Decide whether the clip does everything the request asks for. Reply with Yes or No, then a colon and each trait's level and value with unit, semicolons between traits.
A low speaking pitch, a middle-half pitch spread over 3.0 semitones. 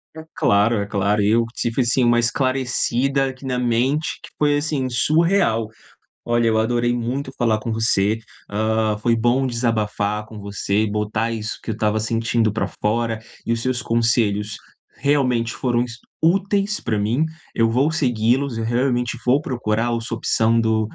No: low, 115 Hz; average, 2.7 semitones